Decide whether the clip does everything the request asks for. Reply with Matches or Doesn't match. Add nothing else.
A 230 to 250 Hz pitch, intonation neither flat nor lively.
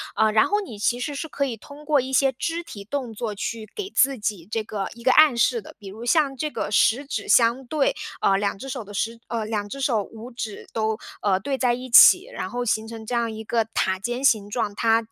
Matches